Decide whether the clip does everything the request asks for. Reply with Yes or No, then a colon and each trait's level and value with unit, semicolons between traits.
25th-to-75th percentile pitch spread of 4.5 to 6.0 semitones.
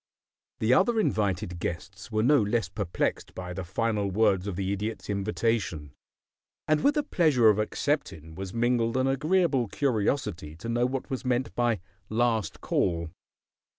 Yes: average, 4.8 semitones